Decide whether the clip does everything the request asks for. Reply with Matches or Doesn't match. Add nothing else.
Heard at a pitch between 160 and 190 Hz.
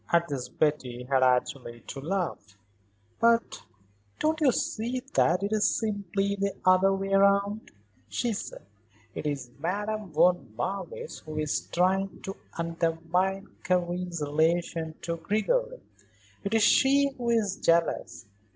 Matches